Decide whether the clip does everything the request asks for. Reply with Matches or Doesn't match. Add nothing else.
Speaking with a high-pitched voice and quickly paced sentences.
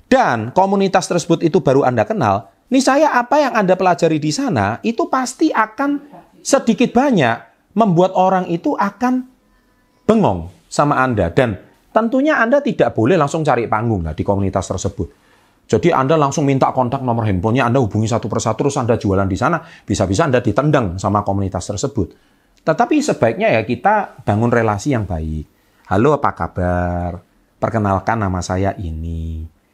Doesn't match